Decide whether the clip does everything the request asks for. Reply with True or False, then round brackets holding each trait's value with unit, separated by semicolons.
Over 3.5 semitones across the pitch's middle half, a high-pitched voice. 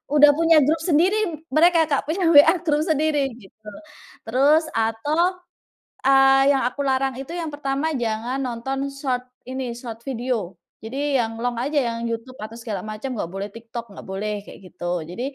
True (4.5 semitones; 265 Hz)